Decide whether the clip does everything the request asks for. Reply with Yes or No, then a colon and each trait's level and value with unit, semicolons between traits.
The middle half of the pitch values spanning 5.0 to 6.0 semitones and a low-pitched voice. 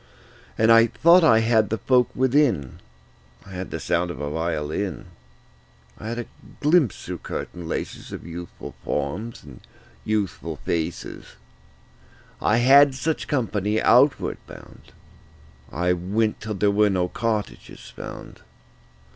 Yes: average, 5.3 semitones; low, 105 Hz